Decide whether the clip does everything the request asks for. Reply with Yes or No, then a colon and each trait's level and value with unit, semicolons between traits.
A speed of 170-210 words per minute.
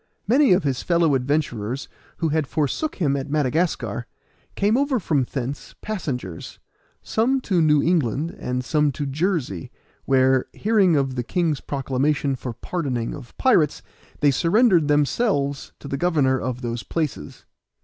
No: average, 145 wpm